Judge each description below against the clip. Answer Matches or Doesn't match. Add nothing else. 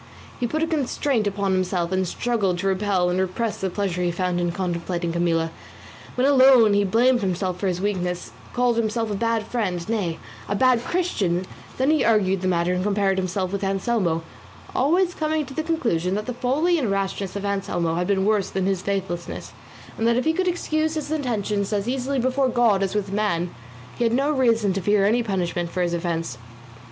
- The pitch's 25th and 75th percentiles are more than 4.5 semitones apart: Matches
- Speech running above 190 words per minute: Matches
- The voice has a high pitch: Matches